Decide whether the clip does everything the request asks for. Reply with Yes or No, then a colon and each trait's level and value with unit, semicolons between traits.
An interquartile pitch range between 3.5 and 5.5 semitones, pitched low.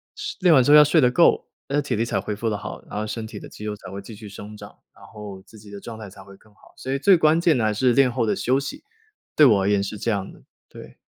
Yes: average, 4.8 semitones; low, 110 Hz